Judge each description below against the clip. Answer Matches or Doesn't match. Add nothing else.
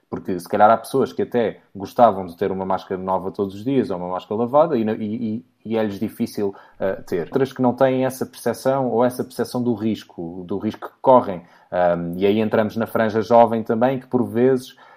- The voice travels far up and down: Doesn't match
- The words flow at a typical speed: Doesn't match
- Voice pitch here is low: Matches